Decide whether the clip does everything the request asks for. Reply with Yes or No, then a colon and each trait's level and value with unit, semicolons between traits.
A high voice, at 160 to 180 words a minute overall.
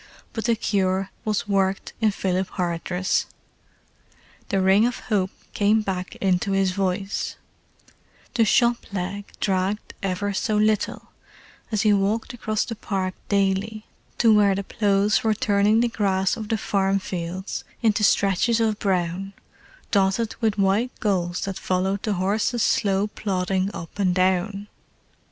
No: high, 200 Hz; average, 140 wpm